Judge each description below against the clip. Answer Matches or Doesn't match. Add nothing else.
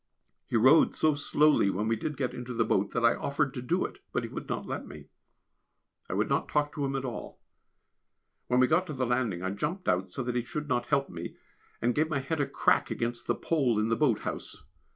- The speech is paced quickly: Matches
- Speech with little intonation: Doesn't match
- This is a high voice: Doesn't match